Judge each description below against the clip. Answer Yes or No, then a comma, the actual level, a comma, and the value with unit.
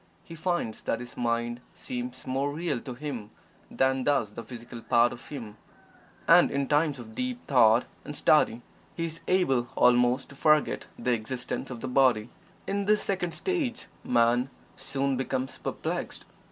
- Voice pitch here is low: Yes, low, 130 Hz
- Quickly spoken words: No, average, 160 wpm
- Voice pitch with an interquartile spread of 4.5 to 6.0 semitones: No, average, 4.0 semitones